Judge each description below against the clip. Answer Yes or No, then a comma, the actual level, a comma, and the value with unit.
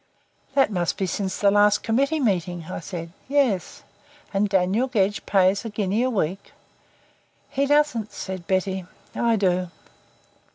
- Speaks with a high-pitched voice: Yes, high, 200 Hz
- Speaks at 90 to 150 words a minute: Yes, average, 140 wpm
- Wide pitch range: No, average, 3.7 semitones